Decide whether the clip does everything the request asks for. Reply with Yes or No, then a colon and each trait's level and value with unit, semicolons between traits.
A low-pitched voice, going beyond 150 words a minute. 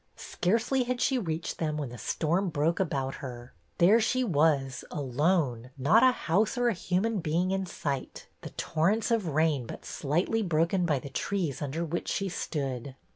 No: medium, 165 Hz; average, 175 wpm